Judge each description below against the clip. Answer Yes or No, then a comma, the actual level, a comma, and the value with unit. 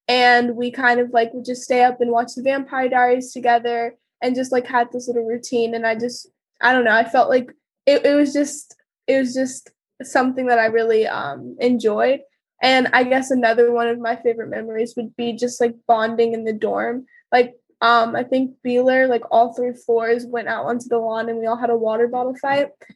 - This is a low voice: No, high, 245 Hz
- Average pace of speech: No, fast, 215 wpm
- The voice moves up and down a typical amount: No, narrow, 1.7 semitones